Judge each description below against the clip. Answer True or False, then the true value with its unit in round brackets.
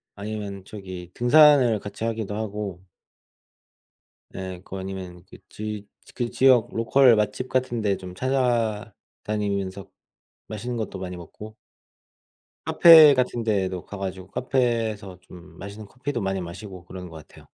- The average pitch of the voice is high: False (105 Hz)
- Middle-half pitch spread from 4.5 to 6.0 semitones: False (3.9 semitones)